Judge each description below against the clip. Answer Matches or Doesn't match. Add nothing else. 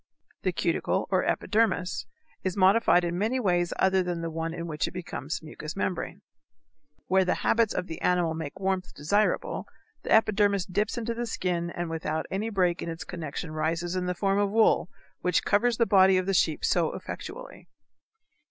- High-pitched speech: Doesn't match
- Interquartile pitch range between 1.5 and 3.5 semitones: Matches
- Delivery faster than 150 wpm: Matches